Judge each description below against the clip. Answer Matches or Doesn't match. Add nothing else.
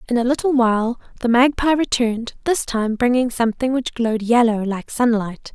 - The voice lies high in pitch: Matches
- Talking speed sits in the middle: Matches